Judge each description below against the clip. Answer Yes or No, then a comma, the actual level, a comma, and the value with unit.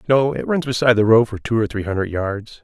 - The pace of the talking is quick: Yes, fast, 275 wpm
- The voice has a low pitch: Yes, low, 115 Hz